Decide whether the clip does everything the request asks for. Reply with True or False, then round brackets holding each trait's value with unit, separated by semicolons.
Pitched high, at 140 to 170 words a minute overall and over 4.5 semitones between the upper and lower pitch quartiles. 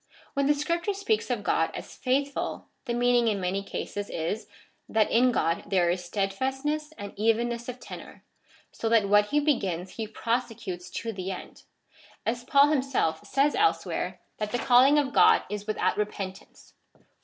True (230 Hz; 165 wpm; 5.3 semitones)